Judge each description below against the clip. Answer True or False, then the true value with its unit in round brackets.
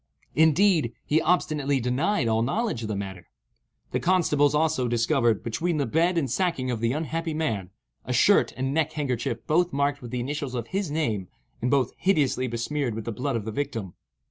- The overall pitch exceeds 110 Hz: True (140 Hz)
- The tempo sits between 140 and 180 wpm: False (190 wpm)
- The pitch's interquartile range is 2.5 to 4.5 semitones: False (5.2 semitones)